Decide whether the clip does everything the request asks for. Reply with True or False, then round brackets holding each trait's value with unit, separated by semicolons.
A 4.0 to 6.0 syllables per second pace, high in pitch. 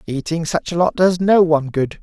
False (5.3 syllables/s; 165 Hz)